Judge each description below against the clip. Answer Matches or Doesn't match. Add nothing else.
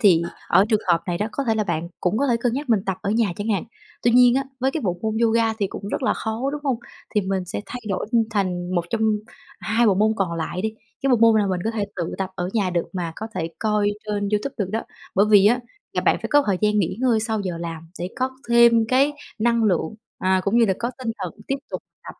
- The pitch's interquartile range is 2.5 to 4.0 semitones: Matches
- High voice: Matches